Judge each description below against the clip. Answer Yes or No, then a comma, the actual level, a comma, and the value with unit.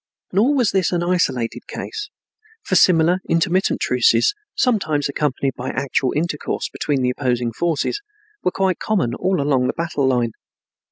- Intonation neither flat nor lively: No, wide, 6.0 semitones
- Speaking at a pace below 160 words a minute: Yes, average, 150 wpm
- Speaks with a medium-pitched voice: Yes, medium, 160 Hz